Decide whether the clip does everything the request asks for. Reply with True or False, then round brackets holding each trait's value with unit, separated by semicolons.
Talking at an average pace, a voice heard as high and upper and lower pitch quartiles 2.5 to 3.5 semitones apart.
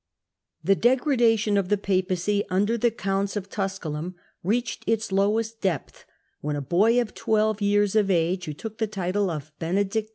True (175 wpm; 200 Hz; 3.0 semitones)